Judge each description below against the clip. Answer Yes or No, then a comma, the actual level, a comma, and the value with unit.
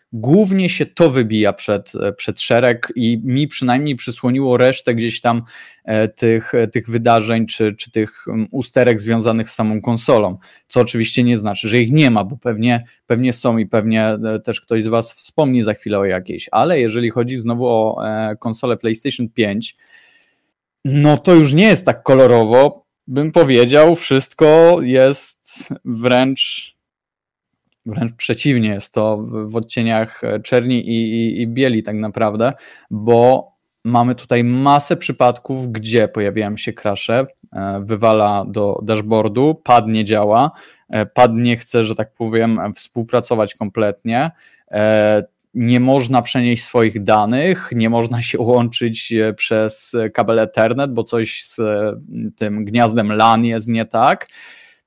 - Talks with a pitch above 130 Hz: No, low, 115 Hz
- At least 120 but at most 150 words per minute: Yes, average, 140 wpm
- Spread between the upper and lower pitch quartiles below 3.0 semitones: Yes, narrow, 2.5 semitones